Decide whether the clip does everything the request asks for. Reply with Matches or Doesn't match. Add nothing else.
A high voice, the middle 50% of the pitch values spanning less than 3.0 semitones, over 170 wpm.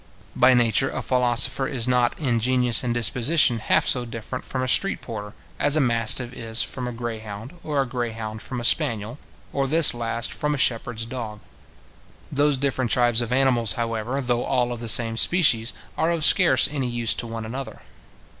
Doesn't match